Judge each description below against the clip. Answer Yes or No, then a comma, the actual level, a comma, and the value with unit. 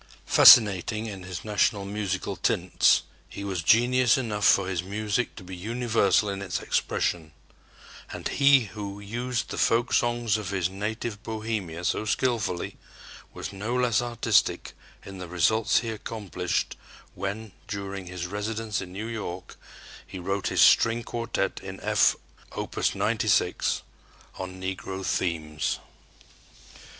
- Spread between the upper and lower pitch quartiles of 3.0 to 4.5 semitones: Yes, average, 3.3 semitones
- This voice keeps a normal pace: No, slow, 130 wpm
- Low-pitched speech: Yes, low, 100 Hz